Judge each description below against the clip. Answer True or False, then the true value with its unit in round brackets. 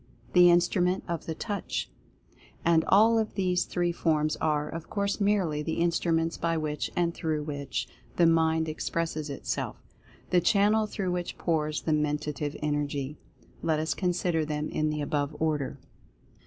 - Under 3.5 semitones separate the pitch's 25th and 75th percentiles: True (2.7 semitones)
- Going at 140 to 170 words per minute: True (155 wpm)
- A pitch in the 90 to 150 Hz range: False (160 Hz)